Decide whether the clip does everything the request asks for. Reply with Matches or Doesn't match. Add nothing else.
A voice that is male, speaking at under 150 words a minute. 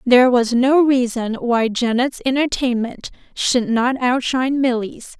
Doesn't match